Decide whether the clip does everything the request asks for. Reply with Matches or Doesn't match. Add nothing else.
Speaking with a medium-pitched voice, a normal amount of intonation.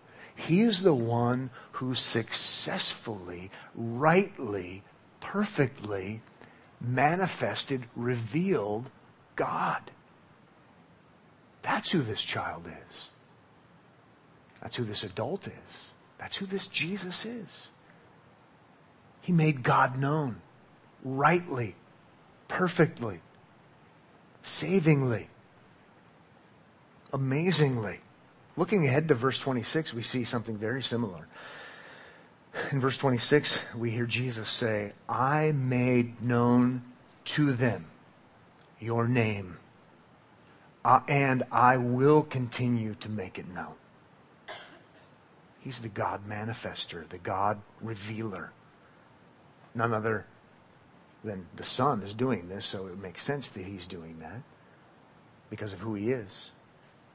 Doesn't match